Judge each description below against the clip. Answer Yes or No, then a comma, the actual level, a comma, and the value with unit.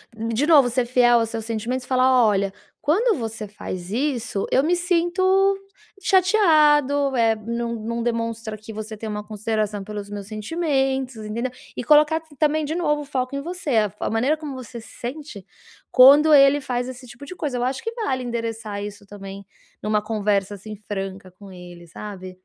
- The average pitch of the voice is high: Yes, high, 235 Hz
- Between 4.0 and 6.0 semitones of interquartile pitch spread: Yes, average, 5.1 semitones